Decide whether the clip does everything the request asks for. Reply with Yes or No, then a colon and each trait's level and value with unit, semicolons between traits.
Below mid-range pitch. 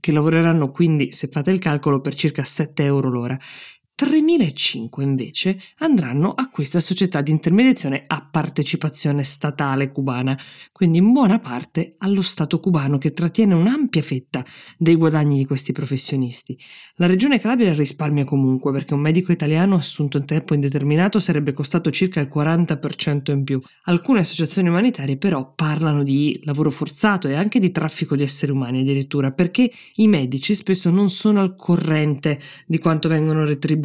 No: medium, 155 Hz